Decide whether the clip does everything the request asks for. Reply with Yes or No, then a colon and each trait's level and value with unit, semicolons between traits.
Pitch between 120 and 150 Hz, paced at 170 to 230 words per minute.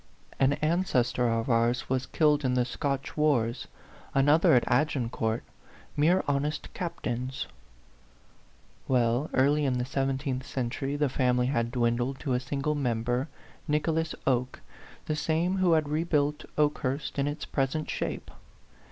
No: low, 135 Hz; slow, 135 wpm